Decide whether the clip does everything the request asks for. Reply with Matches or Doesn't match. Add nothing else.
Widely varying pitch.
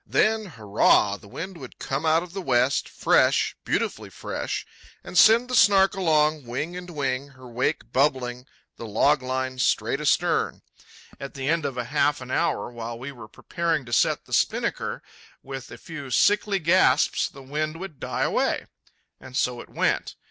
Doesn't match